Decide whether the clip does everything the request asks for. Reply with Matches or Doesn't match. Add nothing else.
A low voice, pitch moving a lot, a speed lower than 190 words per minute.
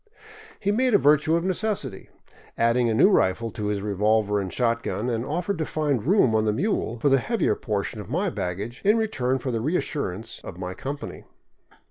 Doesn't match